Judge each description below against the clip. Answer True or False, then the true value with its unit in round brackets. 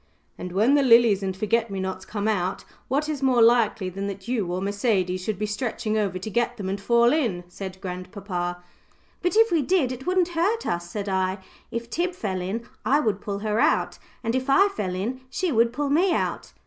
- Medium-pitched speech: False (215 Hz)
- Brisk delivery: True (215 wpm)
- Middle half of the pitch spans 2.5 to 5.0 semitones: False (5.5 semitones)